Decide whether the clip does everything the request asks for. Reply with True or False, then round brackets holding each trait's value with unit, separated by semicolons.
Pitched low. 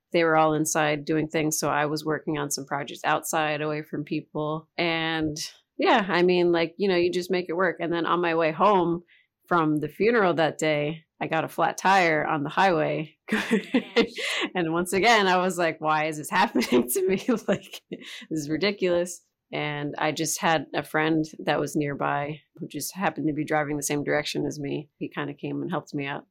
False (160 Hz)